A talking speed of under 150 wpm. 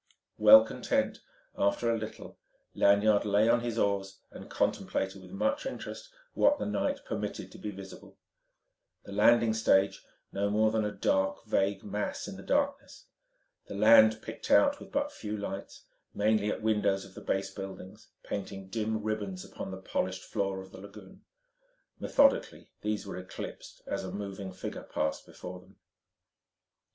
No: average, 160 wpm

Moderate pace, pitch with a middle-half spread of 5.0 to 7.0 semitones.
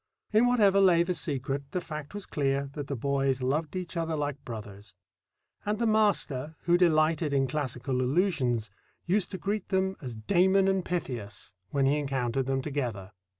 Yes: average, 170 wpm; wide, 5.5 semitones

